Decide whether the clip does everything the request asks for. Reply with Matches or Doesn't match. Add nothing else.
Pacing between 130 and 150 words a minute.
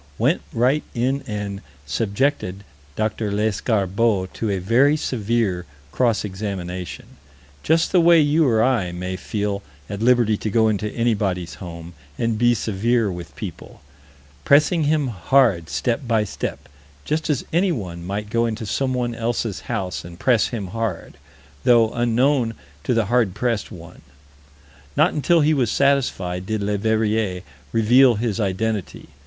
Matches